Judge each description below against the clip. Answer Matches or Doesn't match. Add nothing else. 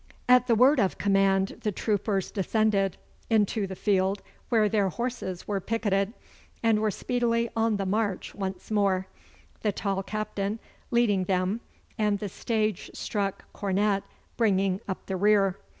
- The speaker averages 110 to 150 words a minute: Matches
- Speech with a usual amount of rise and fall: Doesn't match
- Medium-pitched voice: Doesn't match